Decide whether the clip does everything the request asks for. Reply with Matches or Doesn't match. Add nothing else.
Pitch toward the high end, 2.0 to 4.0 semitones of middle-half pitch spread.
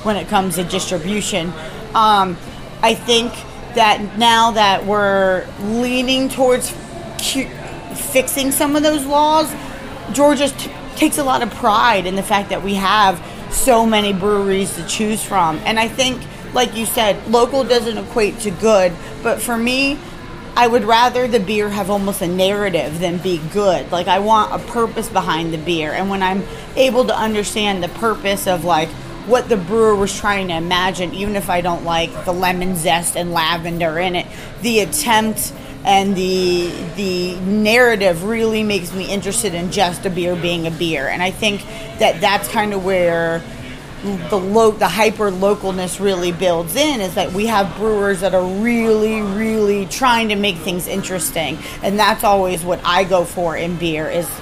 Matches